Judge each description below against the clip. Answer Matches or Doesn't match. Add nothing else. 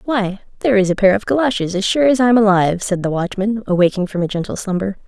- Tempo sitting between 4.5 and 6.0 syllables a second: Doesn't match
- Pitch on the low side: Doesn't match